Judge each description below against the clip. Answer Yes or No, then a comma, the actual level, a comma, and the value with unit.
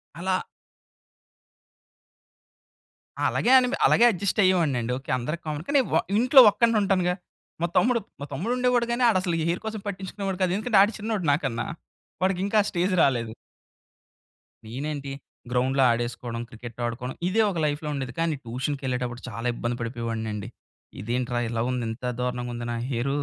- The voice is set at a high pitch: No, medium, 145 Hz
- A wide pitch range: Yes, wide, 8.0 semitones